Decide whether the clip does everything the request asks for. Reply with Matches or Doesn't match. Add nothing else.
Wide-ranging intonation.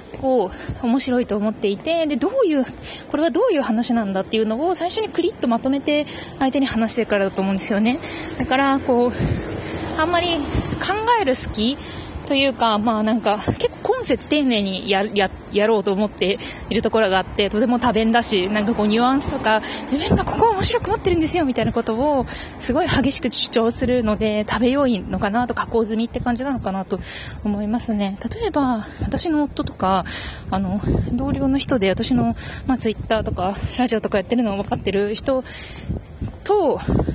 Doesn't match